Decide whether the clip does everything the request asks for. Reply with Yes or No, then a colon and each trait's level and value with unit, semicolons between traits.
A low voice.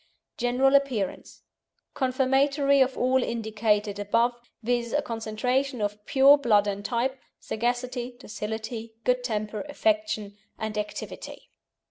No: high, 240 Hz